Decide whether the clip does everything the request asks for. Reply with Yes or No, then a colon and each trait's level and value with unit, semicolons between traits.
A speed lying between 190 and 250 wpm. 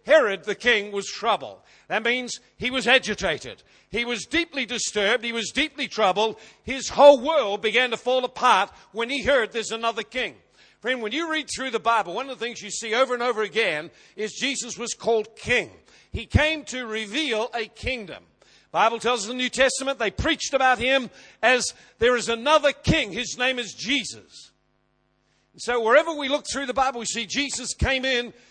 Yes: average, 195 wpm